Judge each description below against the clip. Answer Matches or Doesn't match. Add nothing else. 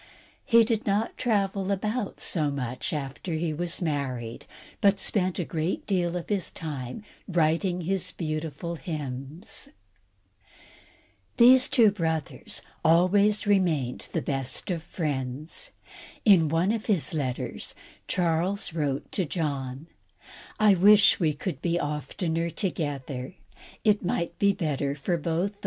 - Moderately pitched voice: Matches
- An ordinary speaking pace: Doesn't match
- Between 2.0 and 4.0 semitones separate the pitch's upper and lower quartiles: Doesn't match